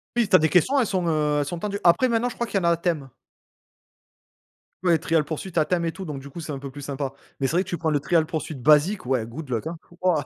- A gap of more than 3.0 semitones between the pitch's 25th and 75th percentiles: Yes, average, 4.0 semitones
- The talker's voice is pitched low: No, medium, 160 Hz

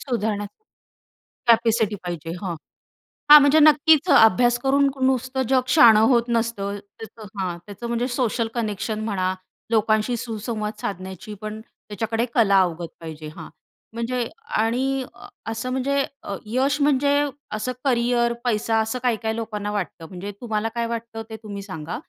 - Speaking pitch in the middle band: No, high, 225 Hz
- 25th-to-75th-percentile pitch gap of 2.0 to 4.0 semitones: Yes, average, 3.1 semitones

